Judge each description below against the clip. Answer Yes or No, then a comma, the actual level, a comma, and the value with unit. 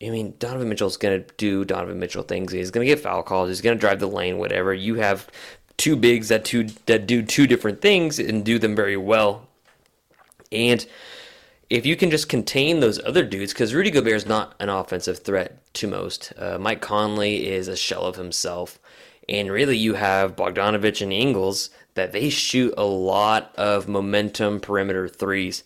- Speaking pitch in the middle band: No, low, 105 Hz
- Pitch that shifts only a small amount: No, average, 3.2 semitones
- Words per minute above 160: Yes, average, 190 wpm